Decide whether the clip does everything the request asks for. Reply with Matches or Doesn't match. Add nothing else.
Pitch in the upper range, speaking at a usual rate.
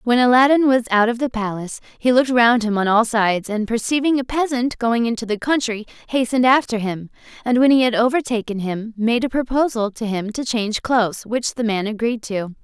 Doesn't match